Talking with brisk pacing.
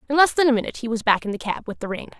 Yes: fast, 385 wpm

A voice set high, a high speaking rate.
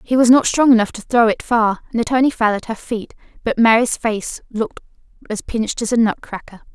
Yes: high, 230 Hz; fast, 220 wpm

